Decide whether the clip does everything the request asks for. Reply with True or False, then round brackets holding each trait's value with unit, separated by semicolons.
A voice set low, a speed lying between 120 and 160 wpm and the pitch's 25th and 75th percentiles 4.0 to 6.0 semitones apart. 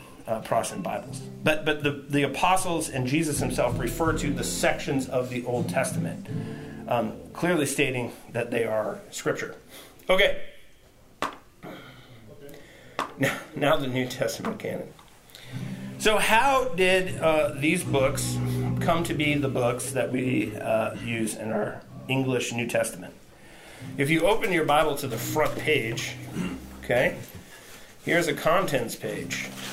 True (130 Hz; 135 wpm; 4.9 semitones)